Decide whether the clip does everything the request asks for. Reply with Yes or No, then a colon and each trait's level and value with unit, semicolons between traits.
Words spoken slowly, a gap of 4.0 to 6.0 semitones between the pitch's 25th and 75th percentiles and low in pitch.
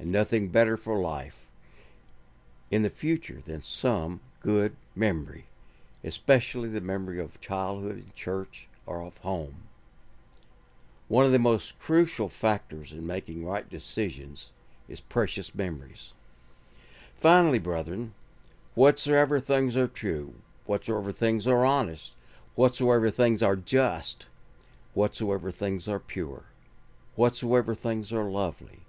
Yes: slow, 120 wpm; wide, 5.6 semitones; low, 105 Hz